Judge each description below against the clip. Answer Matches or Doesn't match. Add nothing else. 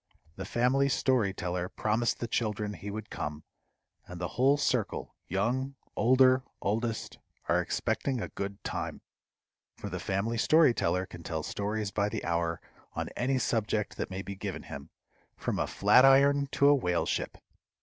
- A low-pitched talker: Matches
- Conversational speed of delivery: Matches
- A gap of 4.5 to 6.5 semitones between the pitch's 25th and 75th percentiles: Matches